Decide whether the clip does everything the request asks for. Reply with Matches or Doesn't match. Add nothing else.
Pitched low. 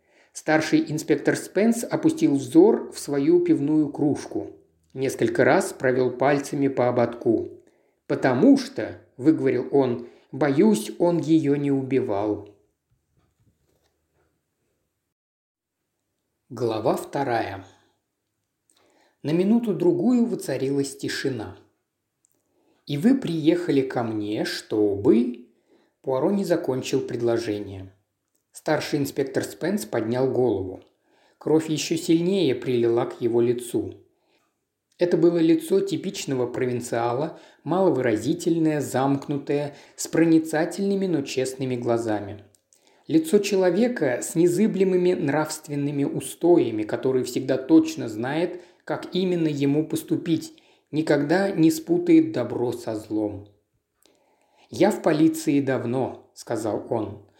Doesn't match